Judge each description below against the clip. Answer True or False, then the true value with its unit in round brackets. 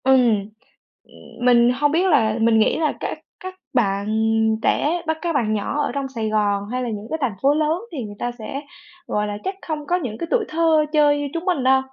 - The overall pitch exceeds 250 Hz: True (270 Hz)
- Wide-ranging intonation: True (6.1 semitones)